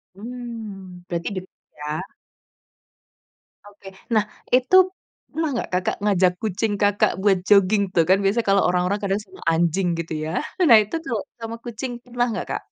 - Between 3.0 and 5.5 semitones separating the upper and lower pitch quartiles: Yes, average, 3.6 semitones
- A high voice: Yes, high, 200 Hz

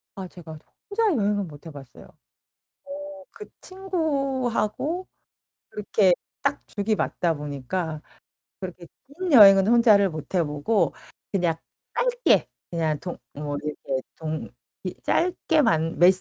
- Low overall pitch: No, high, 190 Hz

